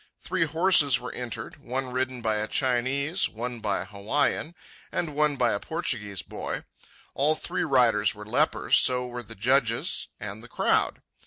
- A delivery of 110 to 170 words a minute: Yes, average, 165 wpm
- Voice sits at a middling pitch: No, low, 125 Hz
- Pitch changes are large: No, average, 4.3 semitones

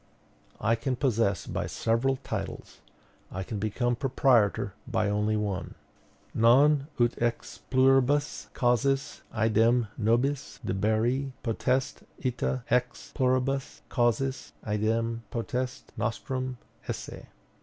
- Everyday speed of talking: No, slow, 100 wpm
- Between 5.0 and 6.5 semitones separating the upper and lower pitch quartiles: No, average, 3.0 semitones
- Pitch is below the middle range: Yes, low, 120 Hz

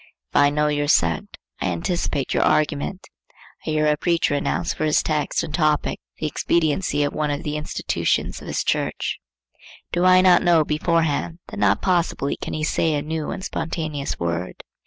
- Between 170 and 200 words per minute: Yes, average, 180 wpm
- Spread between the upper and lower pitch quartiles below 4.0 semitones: Yes, narrow, 2.5 semitones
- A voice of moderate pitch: Yes, medium, 155 Hz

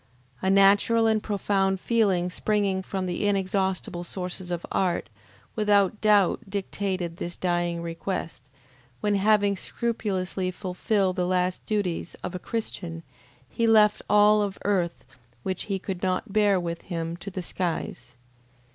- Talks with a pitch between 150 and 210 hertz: Yes, high, 190 Hz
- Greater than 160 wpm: No, average, 140 wpm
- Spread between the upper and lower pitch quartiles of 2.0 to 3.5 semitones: Yes, narrow, 2.4 semitones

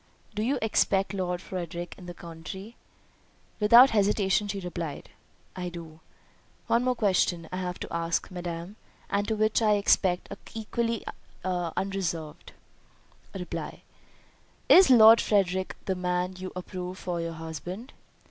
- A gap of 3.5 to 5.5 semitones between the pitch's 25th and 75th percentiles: No, average, 3.1 semitones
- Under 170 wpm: Yes, slow, 135 wpm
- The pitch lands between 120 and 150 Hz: No, medium, 185 Hz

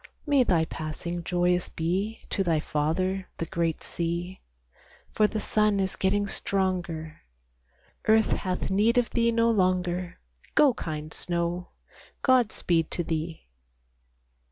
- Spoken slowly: Yes, slow, 130 wpm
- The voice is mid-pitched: Yes, medium, 180 Hz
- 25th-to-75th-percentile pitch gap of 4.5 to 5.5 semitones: No, average, 3.6 semitones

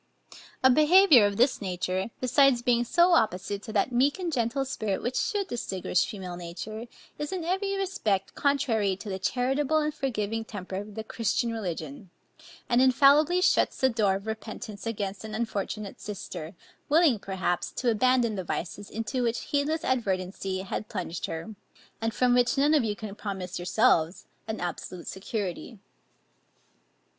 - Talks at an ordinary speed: Yes, average, 155 wpm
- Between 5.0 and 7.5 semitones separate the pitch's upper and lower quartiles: Yes, average, 5.3 semitones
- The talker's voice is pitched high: Yes, high, 220 Hz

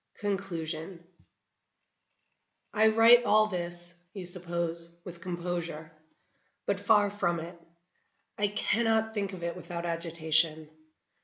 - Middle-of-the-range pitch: Yes, medium, 175 Hz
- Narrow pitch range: No, average, 3.3 semitones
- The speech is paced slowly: Yes, slow, 105 wpm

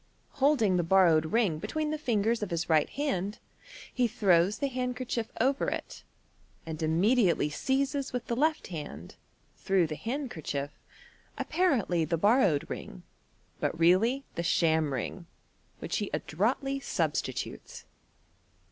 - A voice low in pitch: No, high, 205 Hz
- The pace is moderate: No, slow, 130 wpm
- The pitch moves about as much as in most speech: No, wide, 7.7 semitones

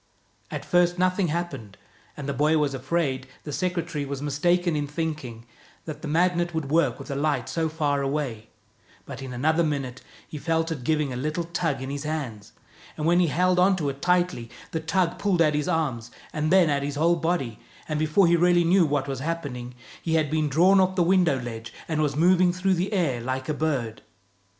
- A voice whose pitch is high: No, medium, 155 Hz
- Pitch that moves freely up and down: No, average, 3.9 semitones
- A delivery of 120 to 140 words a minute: No, fast, 205 wpm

